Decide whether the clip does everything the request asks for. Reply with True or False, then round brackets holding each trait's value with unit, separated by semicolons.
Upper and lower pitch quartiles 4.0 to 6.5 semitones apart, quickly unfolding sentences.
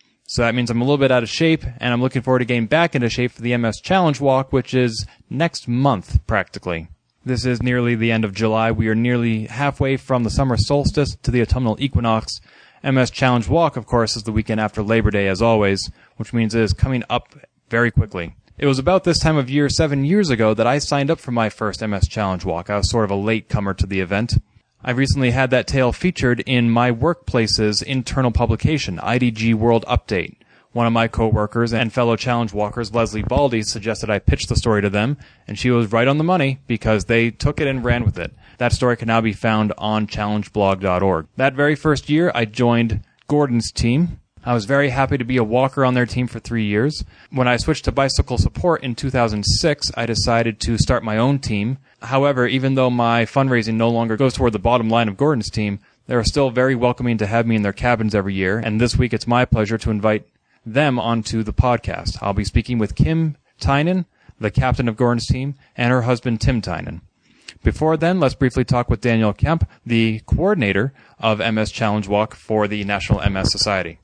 False (3.1 semitones; 215 wpm)